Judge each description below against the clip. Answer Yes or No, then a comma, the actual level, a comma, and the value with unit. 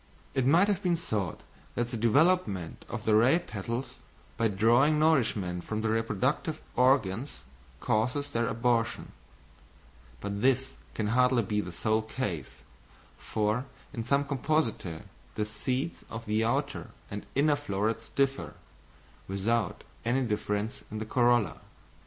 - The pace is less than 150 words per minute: Yes, slow, 135 wpm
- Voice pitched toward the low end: Yes, low, 115 Hz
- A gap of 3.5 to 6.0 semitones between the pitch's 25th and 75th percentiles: Yes, average, 4.2 semitones